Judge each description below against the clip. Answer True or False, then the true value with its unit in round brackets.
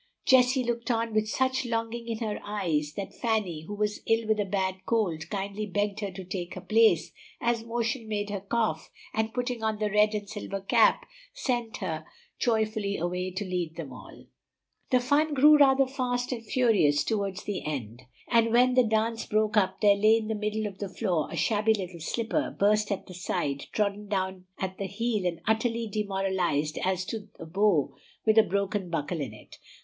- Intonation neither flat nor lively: True (3.3 semitones)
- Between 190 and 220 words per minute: True (195 wpm)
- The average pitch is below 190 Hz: False (210 Hz)